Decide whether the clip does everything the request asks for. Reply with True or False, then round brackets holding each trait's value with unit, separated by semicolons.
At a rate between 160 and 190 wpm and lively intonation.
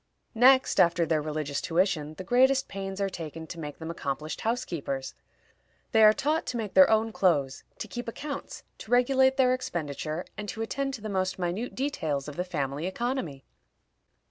True (175 wpm; 7.8 semitones)